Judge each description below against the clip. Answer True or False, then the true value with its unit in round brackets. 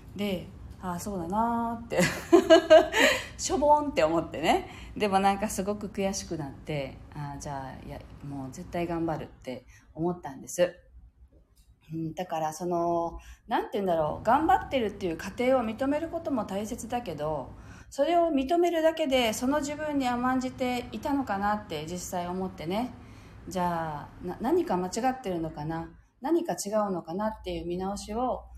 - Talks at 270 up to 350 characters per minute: True (315 characters per minute)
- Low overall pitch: False (195 Hz)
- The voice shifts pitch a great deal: True (7.6 semitones)